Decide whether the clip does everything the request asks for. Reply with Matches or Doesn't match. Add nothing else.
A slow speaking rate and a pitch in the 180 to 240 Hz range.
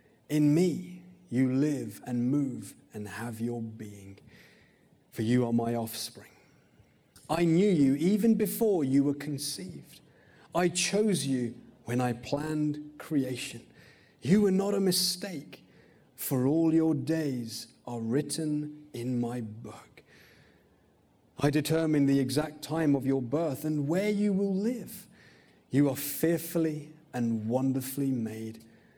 Doesn't match